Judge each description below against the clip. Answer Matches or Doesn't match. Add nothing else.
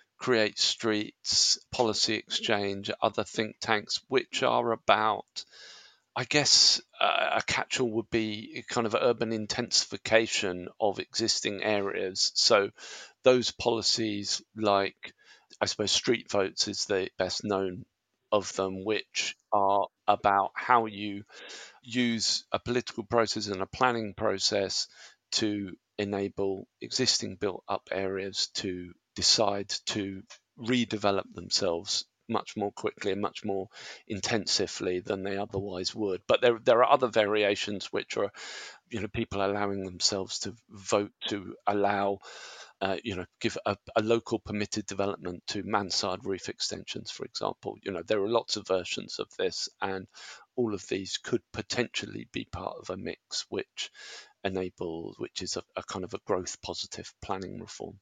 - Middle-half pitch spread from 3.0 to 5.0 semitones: Doesn't match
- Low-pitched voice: Matches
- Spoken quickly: Doesn't match